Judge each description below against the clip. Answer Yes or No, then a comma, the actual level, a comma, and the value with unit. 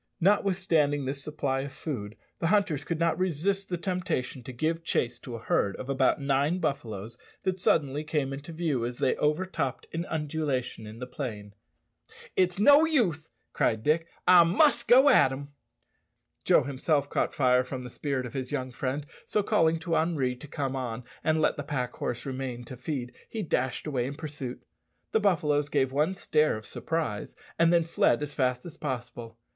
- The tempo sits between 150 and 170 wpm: No, average, 185 wpm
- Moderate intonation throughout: Yes, average, 4.6 semitones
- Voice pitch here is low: No, medium, 145 Hz